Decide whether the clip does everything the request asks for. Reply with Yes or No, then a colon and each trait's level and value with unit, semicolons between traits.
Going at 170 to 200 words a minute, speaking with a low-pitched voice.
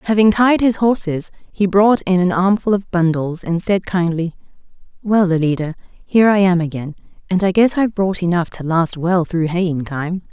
No: average, 185 wpm; medium, 185 Hz